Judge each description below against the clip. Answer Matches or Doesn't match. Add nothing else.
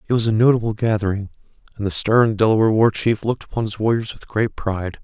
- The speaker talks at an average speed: Doesn't match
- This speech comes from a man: Matches